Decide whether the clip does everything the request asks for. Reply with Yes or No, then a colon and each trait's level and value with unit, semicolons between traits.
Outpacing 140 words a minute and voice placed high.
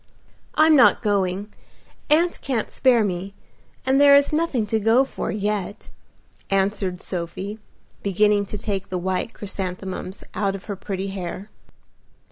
No: slow, 135 wpm; high, 205 Hz